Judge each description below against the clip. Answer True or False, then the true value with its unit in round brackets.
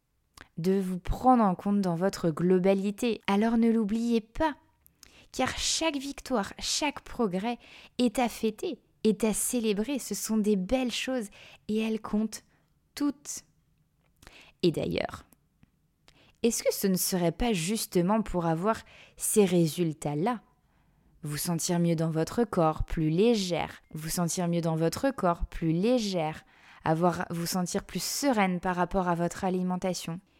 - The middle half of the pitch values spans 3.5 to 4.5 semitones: False (4.9 semitones)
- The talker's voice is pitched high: True (195 Hz)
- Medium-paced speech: False (140 wpm)